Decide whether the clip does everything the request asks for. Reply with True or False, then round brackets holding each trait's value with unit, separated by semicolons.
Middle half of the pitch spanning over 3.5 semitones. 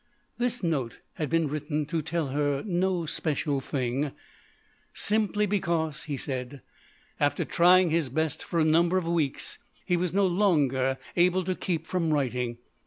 True (3.9 semitones)